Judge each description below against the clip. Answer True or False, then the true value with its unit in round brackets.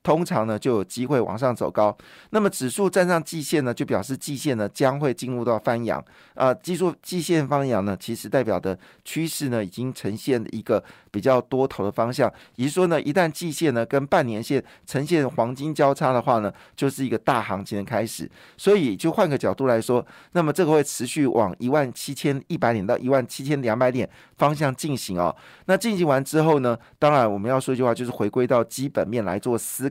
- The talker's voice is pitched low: True (130 Hz)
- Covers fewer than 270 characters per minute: False (320 characters per minute)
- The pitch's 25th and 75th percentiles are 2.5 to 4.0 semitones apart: False (4.7 semitones)